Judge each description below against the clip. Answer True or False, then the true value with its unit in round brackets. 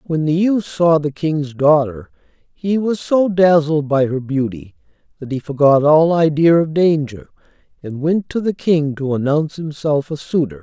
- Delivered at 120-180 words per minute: True (175 wpm)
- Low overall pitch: False (155 Hz)